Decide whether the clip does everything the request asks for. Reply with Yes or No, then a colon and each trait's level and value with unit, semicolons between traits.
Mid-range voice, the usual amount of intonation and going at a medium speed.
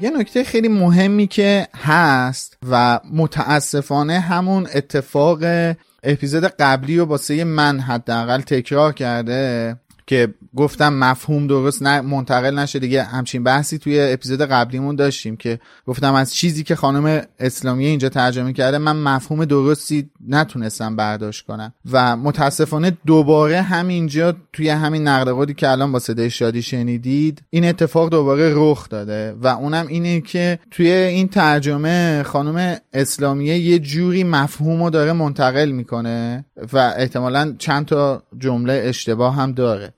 Yes: medium, 145 Hz; average, 3.8 semitones; average, 135 wpm